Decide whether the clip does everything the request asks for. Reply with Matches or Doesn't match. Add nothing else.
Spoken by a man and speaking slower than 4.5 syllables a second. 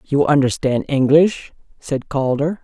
Doesn't match